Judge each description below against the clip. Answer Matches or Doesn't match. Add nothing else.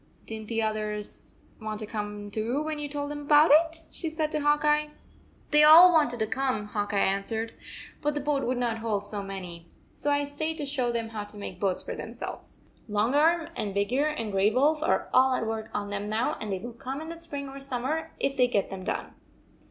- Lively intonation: Matches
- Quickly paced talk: Matches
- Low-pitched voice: Doesn't match